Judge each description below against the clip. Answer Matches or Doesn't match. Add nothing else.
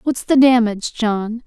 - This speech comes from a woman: Matches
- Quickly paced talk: Doesn't match